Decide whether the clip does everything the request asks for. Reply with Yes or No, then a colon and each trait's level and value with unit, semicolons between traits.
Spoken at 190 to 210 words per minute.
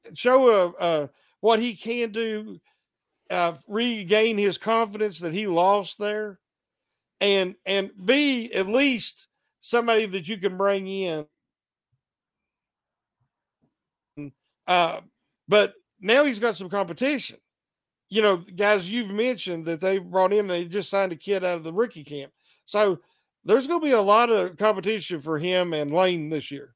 No: average, 155 wpm